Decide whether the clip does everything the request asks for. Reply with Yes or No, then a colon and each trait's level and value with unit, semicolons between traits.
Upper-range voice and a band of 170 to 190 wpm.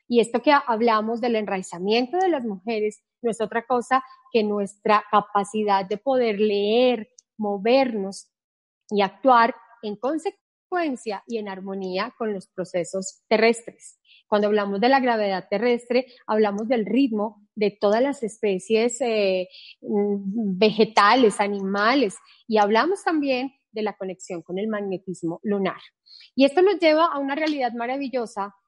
No: high, 220 Hz; average, 135 wpm